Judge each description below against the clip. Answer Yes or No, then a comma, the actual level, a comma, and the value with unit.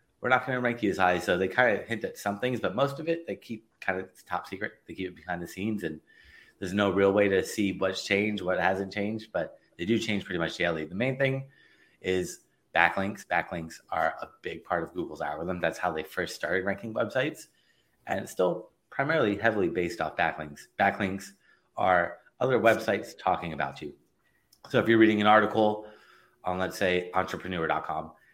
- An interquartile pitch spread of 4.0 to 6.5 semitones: No, average, 2.9 semitones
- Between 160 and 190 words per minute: No, fast, 205 wpm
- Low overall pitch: Yes, low, 100 Hz